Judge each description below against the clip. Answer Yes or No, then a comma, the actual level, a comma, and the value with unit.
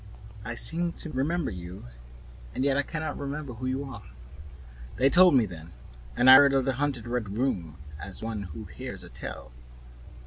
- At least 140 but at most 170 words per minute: No, average, 185 wpm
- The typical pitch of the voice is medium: No, low, 130 Hz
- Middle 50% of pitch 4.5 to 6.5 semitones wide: Yes, average, 5.1 semitones